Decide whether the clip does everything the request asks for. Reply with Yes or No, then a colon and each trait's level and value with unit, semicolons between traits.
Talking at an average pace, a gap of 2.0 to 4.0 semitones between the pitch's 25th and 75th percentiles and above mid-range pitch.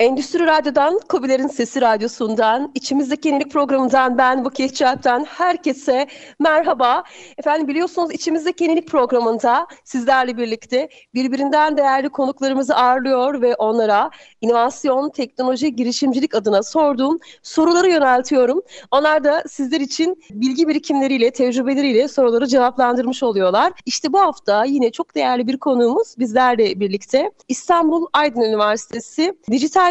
Yes: average, 115 wpm; average, 3.5 semitones; very high, 270 Hz